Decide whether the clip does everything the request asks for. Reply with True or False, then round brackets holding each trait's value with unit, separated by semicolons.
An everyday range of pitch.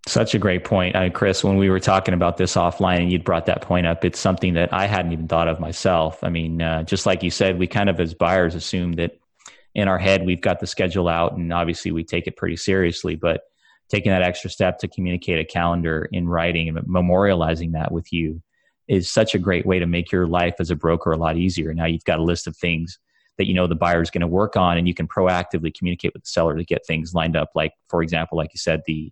False (1.9 semitones)